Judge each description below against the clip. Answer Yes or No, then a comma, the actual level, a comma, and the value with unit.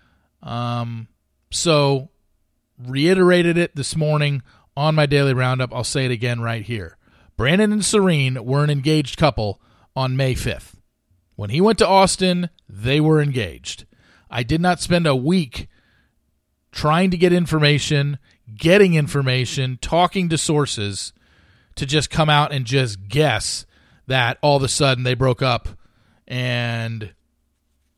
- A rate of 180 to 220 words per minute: No, average, 140 wpm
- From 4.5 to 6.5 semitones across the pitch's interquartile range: Yes, average, 5.1 semitones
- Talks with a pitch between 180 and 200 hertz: No, low, 135 Hz